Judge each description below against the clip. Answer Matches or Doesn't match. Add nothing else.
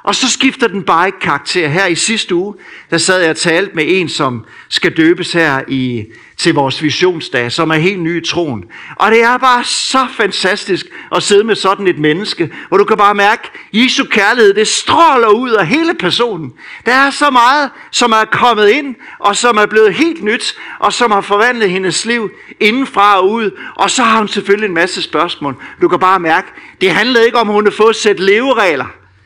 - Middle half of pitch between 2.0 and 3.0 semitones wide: Doesn't match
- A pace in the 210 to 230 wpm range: Matches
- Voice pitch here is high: Matches